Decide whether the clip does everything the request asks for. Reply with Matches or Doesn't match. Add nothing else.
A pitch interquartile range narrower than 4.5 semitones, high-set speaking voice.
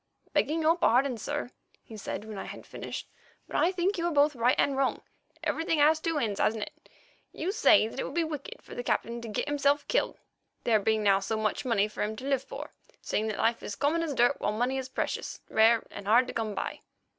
Doesn't match